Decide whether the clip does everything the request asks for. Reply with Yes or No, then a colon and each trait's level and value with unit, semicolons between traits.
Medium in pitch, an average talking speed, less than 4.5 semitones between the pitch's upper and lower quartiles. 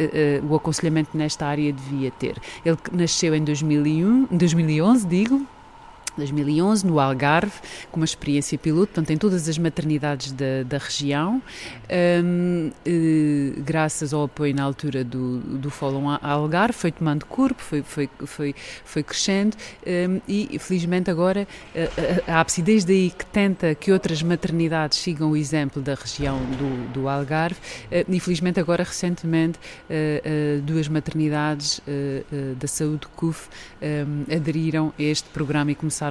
Yes: medium, 155 Hz; average, 135 wpm; average, 3.2 semitones